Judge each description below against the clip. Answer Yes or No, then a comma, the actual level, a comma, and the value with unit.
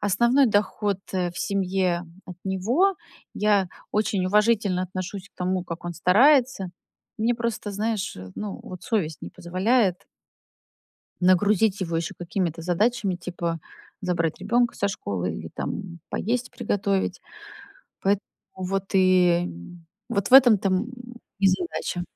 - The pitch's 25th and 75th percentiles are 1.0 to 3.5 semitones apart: Yes, average, 2.9 semitones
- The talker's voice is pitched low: No, high, 195 Hz